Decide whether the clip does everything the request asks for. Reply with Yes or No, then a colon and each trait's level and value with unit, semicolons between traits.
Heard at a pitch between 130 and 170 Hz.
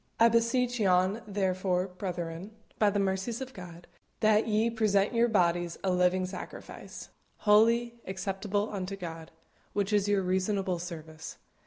No: high, 195 Hz